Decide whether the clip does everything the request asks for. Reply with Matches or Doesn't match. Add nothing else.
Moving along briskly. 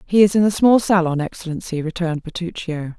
Doesn't match